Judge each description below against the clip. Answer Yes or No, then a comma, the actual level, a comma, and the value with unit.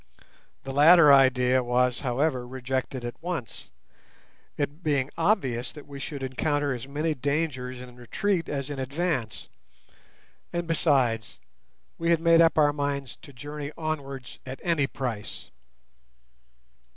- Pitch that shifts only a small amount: No, average, 3.6 semitones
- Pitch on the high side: No, medium, 140 Hz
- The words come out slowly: Yes, slow, 130 wpm